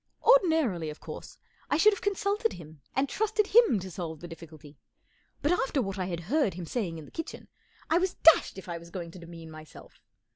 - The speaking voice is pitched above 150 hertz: Yes, high, 190 Hz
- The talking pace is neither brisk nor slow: No, fast, 220 wpm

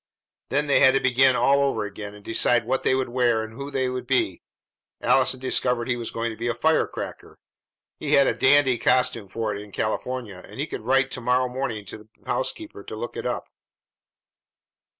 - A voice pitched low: Yes, low, 125 Hz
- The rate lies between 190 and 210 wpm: Yes, fast, 205 wpm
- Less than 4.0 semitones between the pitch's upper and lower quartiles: Yes, average, 2.9 semitones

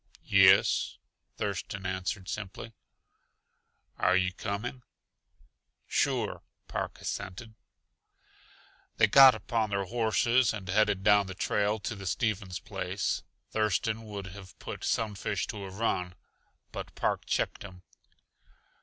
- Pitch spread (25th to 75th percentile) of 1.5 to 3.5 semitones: Yes, average, 2.8 semitones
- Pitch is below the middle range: Yes, low, 100 Hz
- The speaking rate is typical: No, slow, 115 wpm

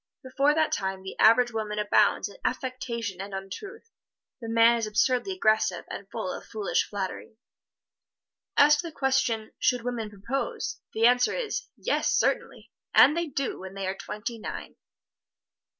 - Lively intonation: No, average, 4.2 semitones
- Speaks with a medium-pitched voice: No, high, 230 Hz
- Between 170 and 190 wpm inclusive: No, average, 155 wpm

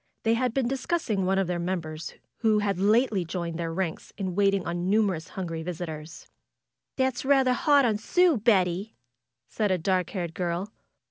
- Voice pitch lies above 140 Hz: Yes, high, 190 Hz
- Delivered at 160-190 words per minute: Yes, average, 175 wpm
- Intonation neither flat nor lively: Yes, average, 4.6 semitones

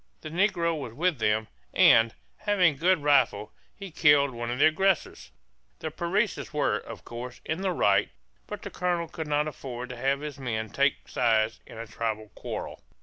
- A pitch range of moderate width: No, wide, 6.1 semitones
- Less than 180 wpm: No, average, 185 wpm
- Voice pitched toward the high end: No, medium, 140 Hz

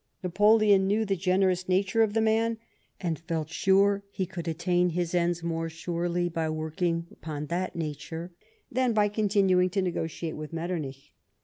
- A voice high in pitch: No, medium, 180 Hz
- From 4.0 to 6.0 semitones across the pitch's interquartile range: No, average, 3.1 semitones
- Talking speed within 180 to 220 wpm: No, average, 165 wpm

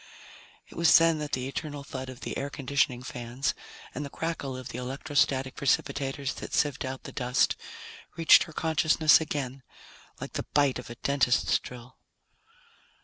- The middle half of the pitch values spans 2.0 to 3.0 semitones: Yes, narrow, 2.5 semitones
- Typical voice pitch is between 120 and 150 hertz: Yes, medium, 140 Hz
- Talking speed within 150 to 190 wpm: Yes, average, 160 wpm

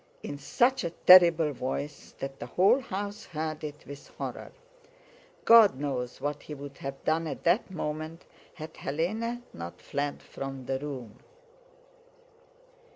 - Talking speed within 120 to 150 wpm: Yes, average, 140 wpm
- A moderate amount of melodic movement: Yes, average, 4.5 semitones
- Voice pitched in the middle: Yes, medium, 150 Hz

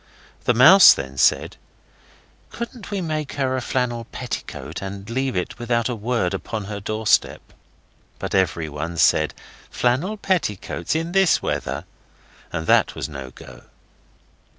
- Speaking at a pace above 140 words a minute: No, slow, 135 wpm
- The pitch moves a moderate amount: No, wide, 8.2 semitones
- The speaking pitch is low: Yes, low, 115 Hz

